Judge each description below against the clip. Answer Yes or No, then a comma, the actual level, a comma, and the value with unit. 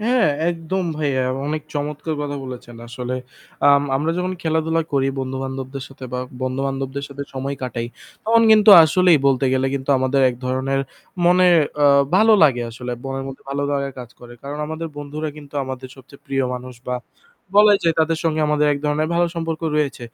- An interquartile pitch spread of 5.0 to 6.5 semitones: No, average, 3.4 semitones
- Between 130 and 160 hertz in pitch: Yes, medium, 140 Hz